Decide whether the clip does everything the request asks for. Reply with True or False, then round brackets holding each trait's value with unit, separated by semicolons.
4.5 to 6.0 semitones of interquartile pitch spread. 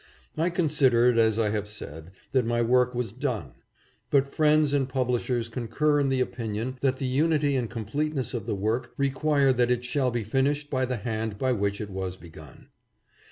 False (3.7 semitones)